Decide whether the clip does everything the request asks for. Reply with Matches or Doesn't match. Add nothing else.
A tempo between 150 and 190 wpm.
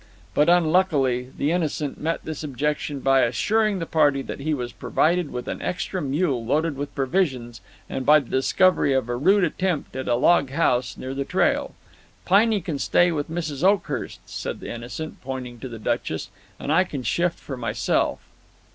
Matches